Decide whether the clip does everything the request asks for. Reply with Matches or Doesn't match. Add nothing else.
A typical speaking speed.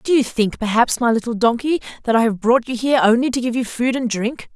Doesn't match